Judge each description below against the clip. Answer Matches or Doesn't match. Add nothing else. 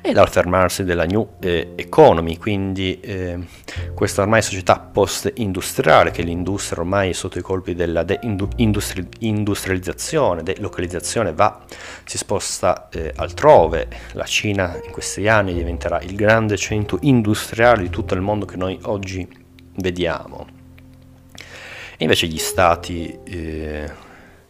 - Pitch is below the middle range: Matches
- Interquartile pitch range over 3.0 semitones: Doesn't match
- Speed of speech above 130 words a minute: Doesn't match